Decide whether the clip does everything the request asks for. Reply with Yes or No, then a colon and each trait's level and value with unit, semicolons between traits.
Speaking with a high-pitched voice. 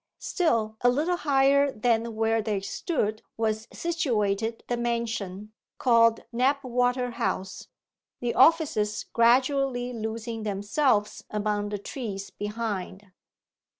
Yes: high, 230 Hz